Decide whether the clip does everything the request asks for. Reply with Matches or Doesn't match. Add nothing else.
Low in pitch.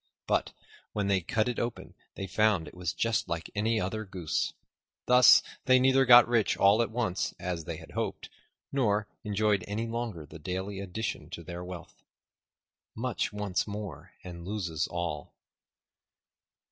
Matches